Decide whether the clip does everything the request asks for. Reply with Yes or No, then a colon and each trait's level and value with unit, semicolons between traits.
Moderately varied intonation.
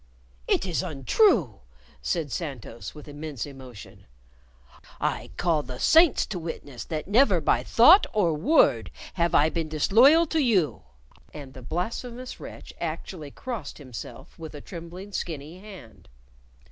No: wide, 6.1 semitones